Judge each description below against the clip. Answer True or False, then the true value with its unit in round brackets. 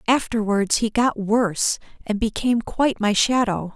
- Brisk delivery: False (145 wpm)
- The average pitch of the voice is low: False (220 Hz)